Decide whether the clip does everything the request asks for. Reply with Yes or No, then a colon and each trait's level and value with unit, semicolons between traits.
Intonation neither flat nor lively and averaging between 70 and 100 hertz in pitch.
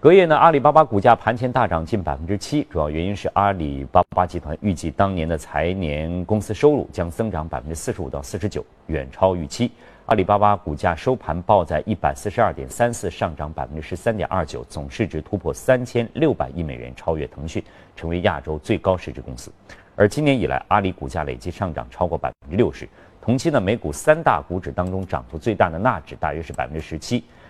No: wide, 5.7 semitones; very low, 95 Hz